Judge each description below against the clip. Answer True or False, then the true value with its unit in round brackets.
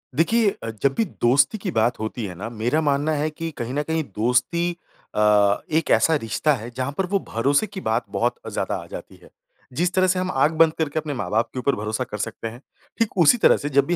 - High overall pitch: False (140 Hz)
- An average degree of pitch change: False (6.2 semitones)